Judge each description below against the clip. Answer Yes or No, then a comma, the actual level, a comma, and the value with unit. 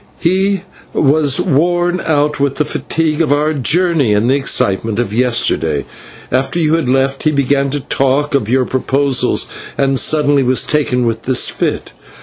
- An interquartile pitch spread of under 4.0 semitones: Yes, average, 3.0 semitones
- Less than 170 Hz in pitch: Yes, medium, 140 Hz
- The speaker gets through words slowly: No, average, 160 wpm